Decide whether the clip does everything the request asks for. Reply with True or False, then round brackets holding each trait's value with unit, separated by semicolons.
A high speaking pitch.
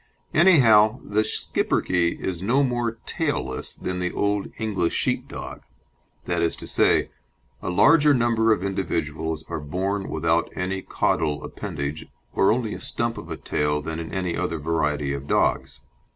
False (95 Hz)